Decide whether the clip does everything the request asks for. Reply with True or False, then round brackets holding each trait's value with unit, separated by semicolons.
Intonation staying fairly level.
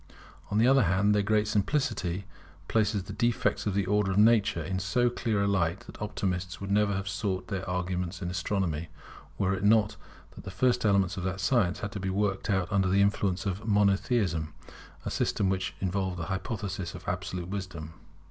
True (2.2 semitones)